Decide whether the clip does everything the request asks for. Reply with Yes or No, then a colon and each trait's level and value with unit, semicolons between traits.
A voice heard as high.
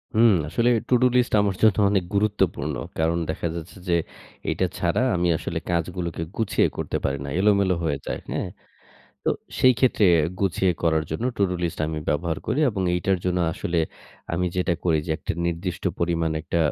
No: very low, 90 Hz